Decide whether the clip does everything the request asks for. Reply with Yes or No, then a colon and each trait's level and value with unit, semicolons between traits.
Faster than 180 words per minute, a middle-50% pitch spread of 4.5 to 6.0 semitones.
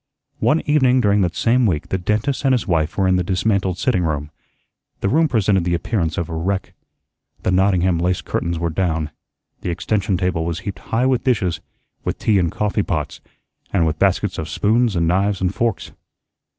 No: average, 190 wpm; average, 4.0 semitones